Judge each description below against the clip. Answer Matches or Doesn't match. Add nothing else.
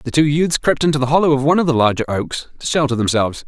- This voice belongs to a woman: Doesn't match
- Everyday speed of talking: Doesn't match